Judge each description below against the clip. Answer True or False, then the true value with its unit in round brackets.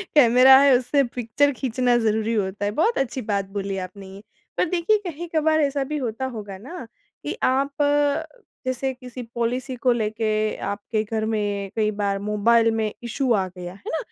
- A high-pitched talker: True (235 Hz)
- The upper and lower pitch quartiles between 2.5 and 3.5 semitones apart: False (4.1 semitones)